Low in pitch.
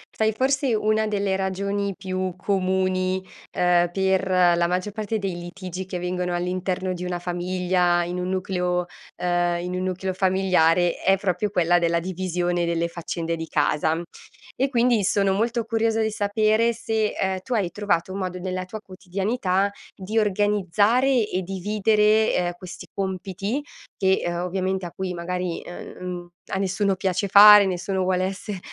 No: medium, 185 Hz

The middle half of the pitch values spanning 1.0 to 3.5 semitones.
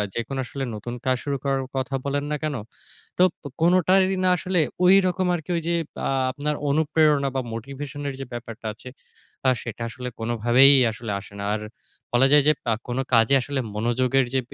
No: average, 4.0 semitones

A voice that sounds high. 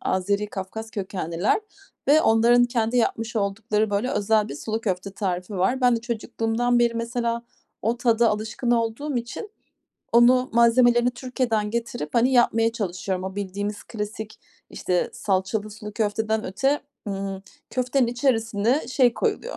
Yes: high, 225 Hz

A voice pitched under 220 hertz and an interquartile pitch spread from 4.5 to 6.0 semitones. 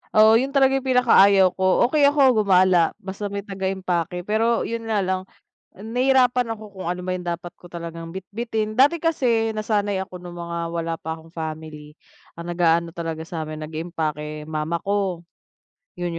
Yes: high, 190 Hz; average, 4.8 semitones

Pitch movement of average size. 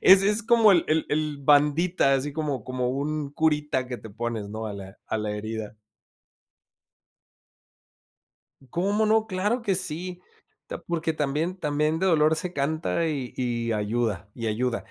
No: wide, 6.2 semitones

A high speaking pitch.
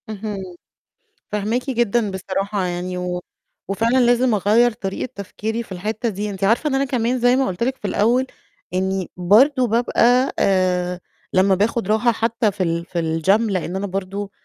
Yes: high, 205 Hz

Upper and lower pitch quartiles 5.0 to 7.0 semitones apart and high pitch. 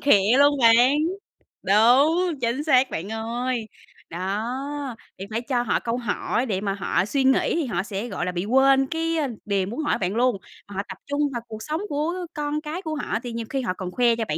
Yes: wide, 5.4 semitones; high, 245 Hz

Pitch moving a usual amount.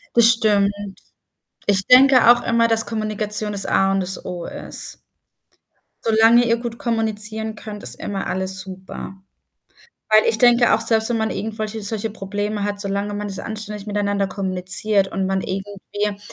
No: narrow, 2.1 semitones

